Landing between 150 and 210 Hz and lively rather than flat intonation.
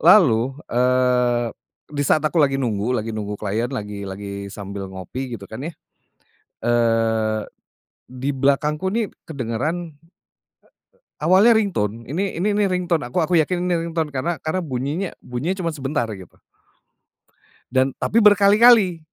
No: low, 135 Hz; wide, 7.3 semitones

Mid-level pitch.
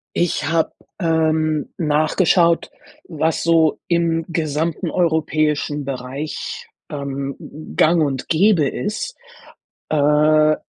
Yes: medium, 155 Hz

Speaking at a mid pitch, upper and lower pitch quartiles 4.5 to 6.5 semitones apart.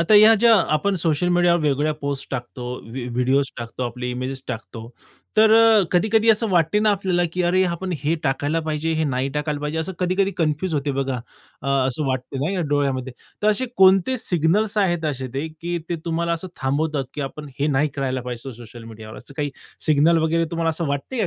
Yes: medium, 155 Hz; average, 4.8 semitones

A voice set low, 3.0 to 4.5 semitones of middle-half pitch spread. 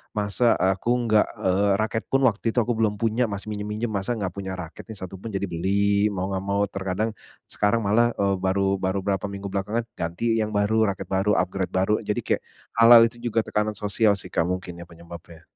No: low, 100 Hz; narrow, 2.5 semitones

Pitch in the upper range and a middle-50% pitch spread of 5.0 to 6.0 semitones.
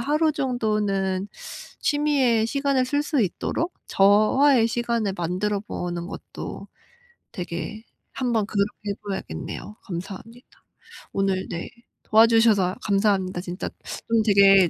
No: high, 210 Hz; average, 3.7 semitones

